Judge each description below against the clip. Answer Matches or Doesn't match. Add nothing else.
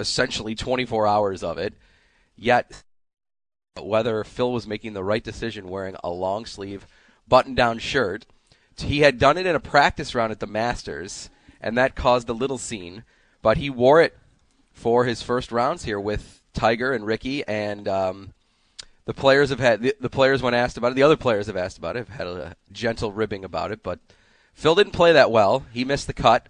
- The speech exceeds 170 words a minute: Matches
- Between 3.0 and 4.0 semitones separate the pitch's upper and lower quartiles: Matches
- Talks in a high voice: Doesn't match